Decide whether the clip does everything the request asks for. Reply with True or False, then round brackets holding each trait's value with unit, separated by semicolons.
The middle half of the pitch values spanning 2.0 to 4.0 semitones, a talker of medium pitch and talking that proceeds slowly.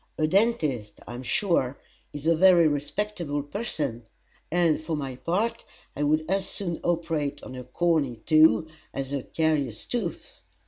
False (3.7 semitones; 155 Hz; 150 wpm)